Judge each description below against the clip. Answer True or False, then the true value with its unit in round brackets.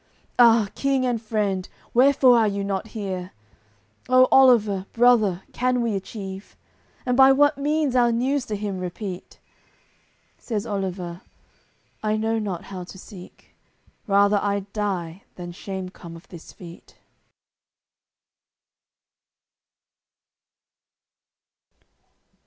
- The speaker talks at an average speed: False (110 wpm)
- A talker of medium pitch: False (210 Hz)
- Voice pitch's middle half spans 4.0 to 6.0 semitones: True (4.3 semitones)